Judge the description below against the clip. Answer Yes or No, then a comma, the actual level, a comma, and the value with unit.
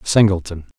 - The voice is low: Yes, very low, 90 Hz